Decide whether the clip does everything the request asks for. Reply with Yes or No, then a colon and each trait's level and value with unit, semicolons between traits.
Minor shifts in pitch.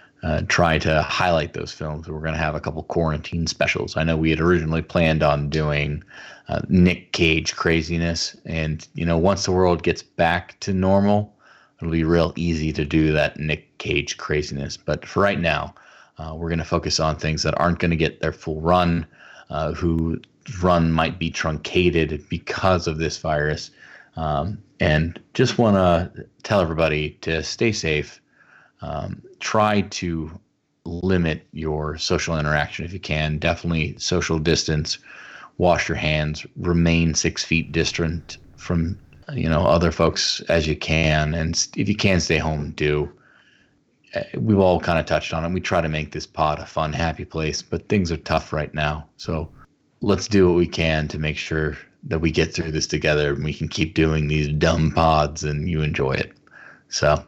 Yes: narrow, 2.1 semitones